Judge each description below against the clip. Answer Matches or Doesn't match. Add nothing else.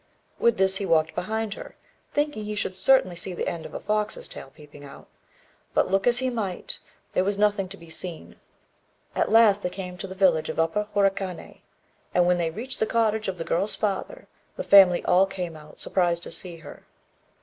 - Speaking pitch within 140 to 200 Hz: Matches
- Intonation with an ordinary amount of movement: Matches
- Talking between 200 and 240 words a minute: Matches